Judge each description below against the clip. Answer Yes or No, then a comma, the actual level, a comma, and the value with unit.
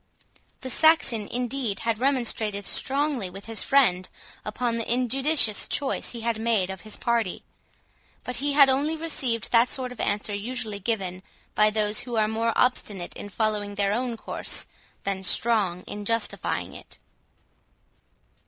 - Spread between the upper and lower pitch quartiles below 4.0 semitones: Yes, average, 3.5 semitones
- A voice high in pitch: Yes, high, 230 Hz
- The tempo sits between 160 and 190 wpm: No, average, 150 wpm